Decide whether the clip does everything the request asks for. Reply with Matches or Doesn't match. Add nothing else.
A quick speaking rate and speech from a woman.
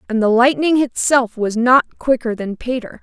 Doesn't match